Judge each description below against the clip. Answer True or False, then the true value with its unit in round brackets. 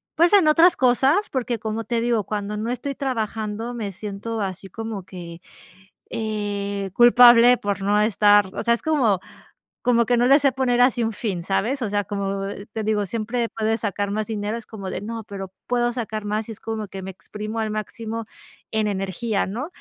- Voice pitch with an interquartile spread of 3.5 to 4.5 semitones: False (2.8 semitones)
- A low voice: False (220 Hz)